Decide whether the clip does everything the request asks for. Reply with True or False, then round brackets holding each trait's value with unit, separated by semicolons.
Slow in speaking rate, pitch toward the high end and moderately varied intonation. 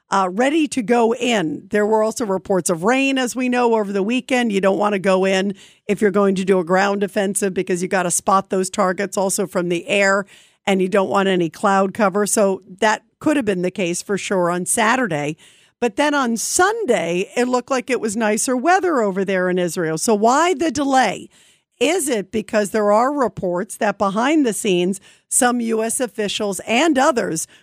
False (205 wpm; 205 Hz; 4.0 semitones)